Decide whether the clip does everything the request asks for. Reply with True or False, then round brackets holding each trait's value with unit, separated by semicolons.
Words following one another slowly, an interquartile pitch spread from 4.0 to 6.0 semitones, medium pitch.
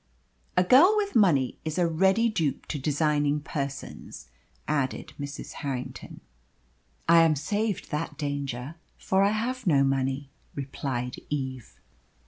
True (125 wpm; 5.3 semitones; 150 Hz)